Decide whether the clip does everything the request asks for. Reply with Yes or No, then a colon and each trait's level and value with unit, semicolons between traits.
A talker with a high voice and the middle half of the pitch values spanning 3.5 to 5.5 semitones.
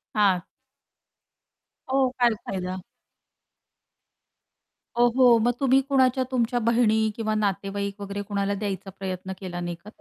Yes: high, 205 Hz; average, 3.8 semitones